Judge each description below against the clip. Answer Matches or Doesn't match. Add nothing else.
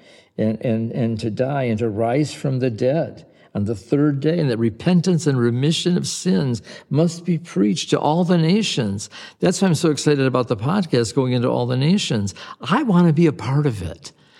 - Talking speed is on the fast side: Matches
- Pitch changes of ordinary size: Doesn't match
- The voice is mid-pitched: Matches